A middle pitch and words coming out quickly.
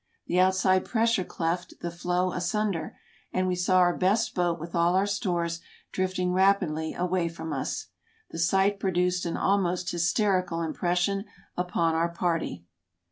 No: medium, 180 Hz; average, 145 wpm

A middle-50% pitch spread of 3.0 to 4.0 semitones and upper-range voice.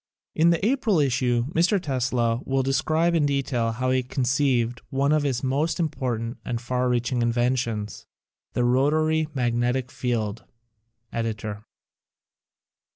No: average, 3.4 semitones; low, 130 Hz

